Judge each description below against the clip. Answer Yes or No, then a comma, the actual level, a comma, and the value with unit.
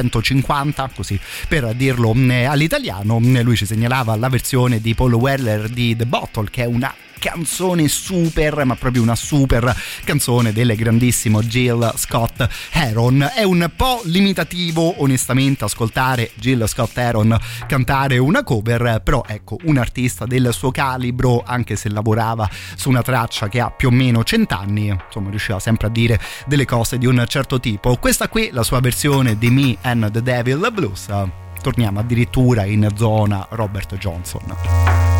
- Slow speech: No, average, 155 wpm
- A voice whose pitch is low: Yes, low, 120 Hz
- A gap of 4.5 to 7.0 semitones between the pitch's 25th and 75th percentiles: No, average, 3.3 semitones